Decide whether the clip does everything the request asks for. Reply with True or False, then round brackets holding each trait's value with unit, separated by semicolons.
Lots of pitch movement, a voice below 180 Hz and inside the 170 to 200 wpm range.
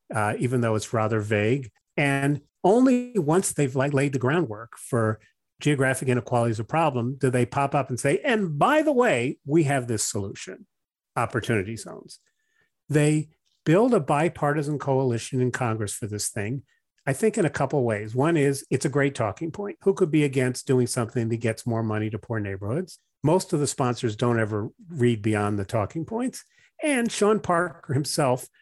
True (6.2 semitones; 135 Hz; 180 wpm)